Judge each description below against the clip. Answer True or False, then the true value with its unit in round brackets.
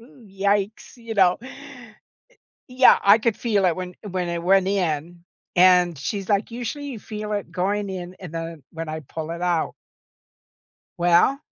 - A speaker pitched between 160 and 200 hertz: True (190 Hz)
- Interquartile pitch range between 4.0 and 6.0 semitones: False (3.5 semitones)